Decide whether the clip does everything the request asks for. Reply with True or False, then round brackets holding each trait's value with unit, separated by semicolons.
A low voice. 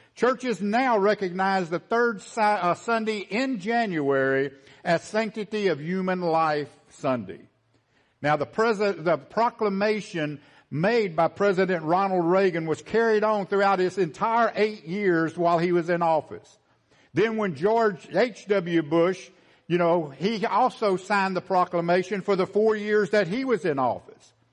False (195 Hz)